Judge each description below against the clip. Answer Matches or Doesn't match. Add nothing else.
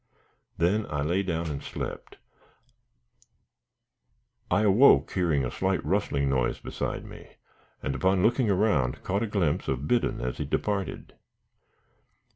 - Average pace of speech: Doesn't match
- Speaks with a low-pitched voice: Matches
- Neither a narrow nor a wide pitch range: Doesn't match